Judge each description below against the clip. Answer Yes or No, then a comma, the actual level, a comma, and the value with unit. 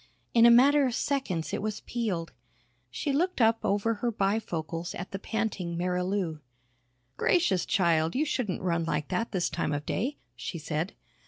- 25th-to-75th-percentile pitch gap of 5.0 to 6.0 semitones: Yes, wide, 5.6 semitones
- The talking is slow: No, average, 165 wpm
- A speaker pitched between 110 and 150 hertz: No, high, 195 Hz